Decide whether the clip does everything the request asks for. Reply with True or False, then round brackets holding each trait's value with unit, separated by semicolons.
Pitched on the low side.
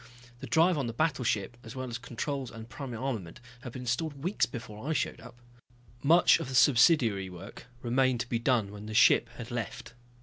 True (120 Hz)